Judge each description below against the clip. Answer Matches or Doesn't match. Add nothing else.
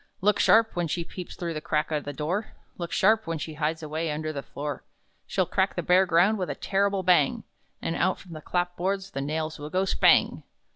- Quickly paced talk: Matches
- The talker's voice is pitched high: Doesn't match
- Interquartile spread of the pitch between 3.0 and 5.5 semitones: Matches